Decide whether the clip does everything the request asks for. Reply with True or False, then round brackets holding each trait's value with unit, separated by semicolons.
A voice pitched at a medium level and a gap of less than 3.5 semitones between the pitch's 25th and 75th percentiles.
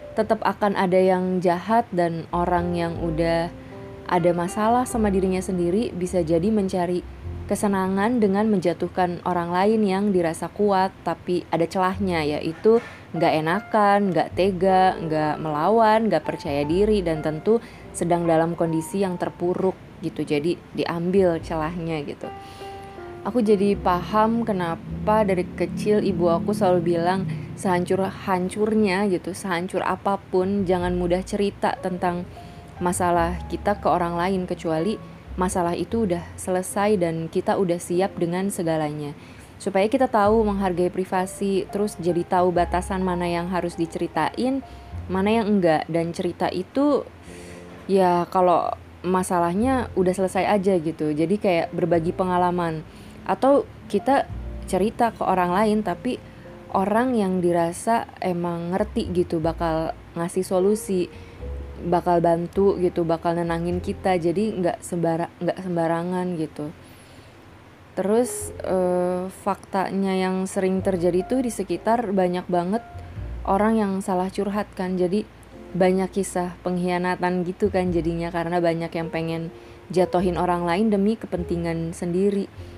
True (180 Hz; 2.5 semitones)